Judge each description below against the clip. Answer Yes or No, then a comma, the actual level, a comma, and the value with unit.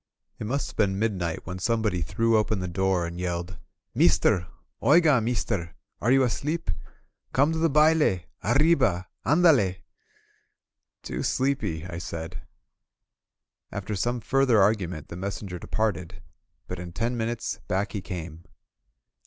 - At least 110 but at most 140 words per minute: Yes, slow, 135 wpm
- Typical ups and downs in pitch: No, wide, 5.8 semitones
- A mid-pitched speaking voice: No, low, 100 Hz